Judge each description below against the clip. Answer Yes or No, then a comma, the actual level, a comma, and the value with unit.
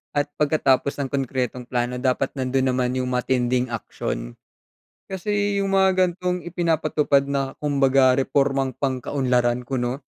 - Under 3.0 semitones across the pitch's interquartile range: Yes, narrow, 2.6 semitones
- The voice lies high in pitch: No, low, 135 Hz